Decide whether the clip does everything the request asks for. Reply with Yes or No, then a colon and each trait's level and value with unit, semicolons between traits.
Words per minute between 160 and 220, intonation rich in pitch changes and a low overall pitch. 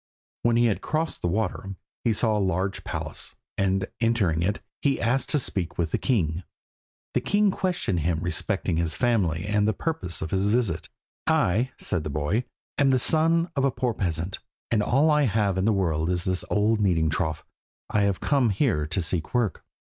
Yes: average, 195 wpm; wide, 5.7 semitones; low, 100 Hz